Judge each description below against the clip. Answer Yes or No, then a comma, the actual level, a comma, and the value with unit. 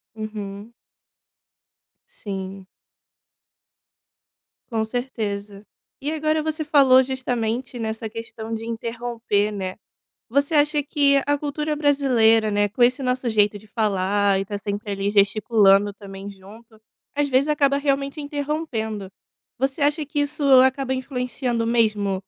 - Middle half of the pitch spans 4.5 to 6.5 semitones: Yes, average, 5.2 semitones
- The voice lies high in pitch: Yes, high, 230 Hz